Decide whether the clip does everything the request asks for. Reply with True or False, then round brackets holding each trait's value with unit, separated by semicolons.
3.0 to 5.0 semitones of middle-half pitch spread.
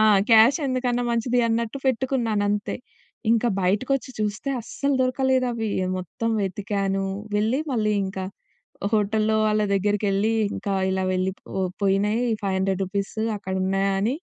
True (3.3 semitones)